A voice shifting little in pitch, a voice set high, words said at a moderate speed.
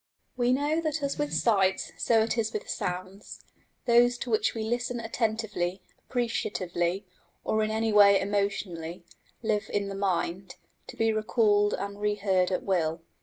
No: average, 3.1 semitones; high, 210 Hz; average, 155 wpm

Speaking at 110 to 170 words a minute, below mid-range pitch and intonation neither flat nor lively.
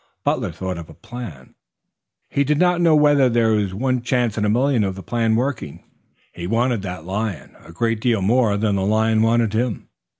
No: average, 200 wpm; low, 110 Hz; average, 4.0 semitones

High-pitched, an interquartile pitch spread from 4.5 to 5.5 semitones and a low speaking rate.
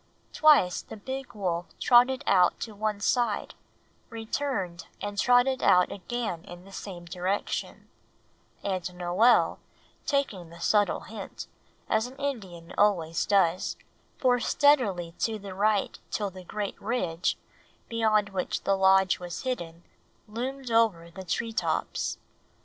Yes: high, 205 Hz; average, 4.9 semitones; slow, 130 wpm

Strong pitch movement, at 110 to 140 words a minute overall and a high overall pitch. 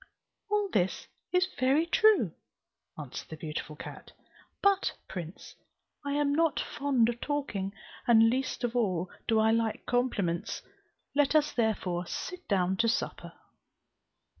Yes: wide, 7.2 semitones; slow, 135 wpm; high, 235 Hz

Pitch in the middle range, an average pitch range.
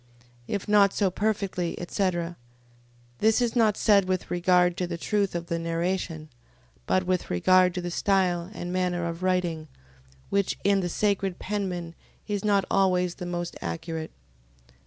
No: medium, 180 Hz; narrow, 2.3 semitones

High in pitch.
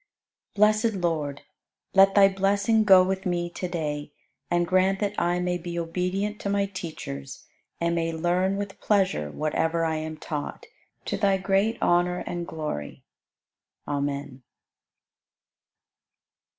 No: medium, 180 Hz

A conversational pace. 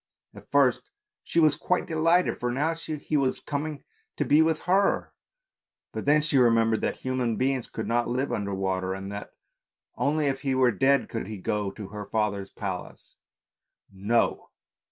Yes: average, 175 wpm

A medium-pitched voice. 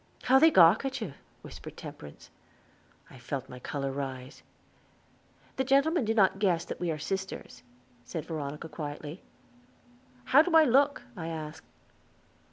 Yes: medium, 165 Hz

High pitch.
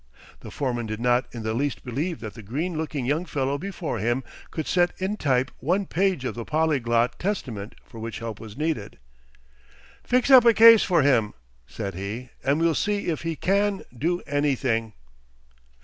No: medium, 140 Hz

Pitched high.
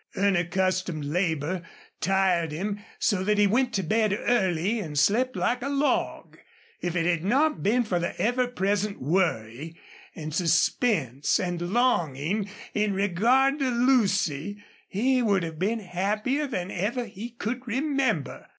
Yes: high, 200 Hz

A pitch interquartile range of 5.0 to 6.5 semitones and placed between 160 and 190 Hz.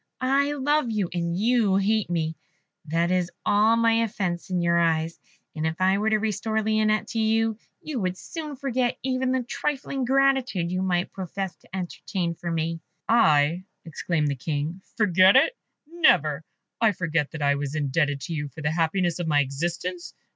Yes: wide, 5.5 semitones; medium, 185 Hz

